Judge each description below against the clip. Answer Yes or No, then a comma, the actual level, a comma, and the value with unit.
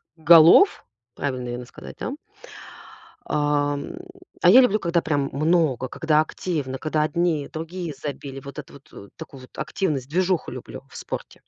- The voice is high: No, medium, 150 Hz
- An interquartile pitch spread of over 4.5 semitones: No, average, 3.4 semitones